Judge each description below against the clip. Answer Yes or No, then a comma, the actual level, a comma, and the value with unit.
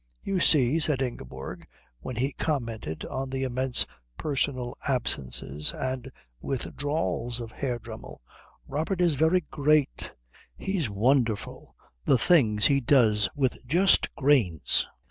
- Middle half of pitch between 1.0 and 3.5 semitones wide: No, average, 4.3 semitones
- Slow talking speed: Yes, slow, 120 wpm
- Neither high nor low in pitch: No, low, 130 Hz